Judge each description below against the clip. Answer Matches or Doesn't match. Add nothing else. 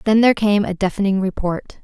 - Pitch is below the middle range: Doesn't match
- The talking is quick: Doesn't match